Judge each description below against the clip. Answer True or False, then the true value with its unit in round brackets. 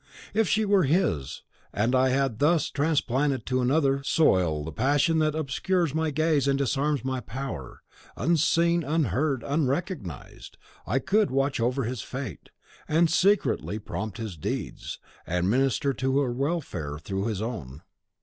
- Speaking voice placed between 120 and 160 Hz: True (135 Hz)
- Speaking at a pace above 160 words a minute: False (145 wpm)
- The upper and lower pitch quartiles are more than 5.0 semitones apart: True (5.4 semitones)